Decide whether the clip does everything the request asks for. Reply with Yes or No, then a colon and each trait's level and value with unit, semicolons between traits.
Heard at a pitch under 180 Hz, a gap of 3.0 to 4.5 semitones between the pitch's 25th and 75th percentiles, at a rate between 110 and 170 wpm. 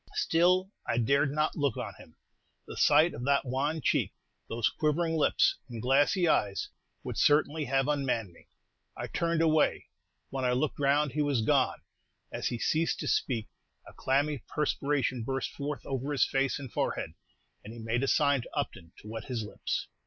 No: medium, 140 Hz; average, 3.6 semitones; average, 180 wpm